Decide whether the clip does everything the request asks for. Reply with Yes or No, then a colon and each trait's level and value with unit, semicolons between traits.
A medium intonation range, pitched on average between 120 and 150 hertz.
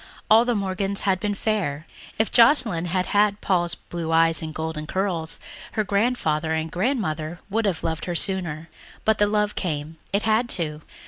No: average, 4.5 semitones; medium, 185 Hz